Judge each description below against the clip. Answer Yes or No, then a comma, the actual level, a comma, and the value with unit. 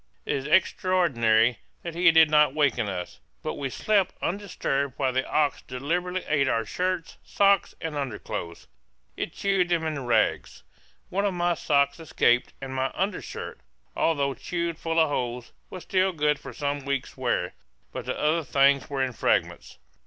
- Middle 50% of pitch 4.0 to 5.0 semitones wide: Yes, average, 4.7 semitones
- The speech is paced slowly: No, average, 165 wpm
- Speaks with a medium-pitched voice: Yes, medium, 150 Hz